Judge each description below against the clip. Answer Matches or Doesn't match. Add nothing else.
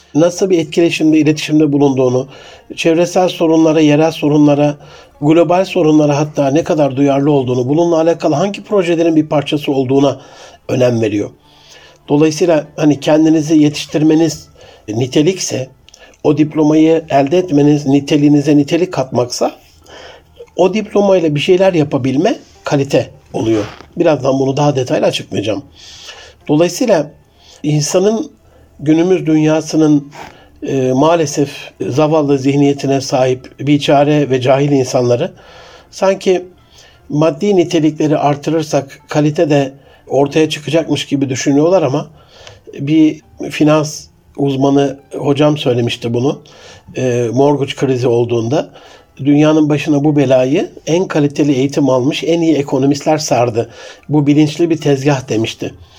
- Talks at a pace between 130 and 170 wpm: Doesn't match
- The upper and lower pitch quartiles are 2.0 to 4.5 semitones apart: Matches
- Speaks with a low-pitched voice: Doesn't match